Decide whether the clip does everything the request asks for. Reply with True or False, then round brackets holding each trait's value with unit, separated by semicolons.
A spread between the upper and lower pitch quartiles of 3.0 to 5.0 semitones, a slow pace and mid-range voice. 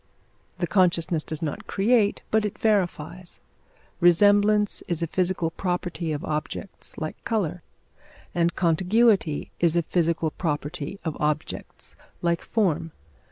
True (3.6 semitones; 120 wpm; 175 Hz)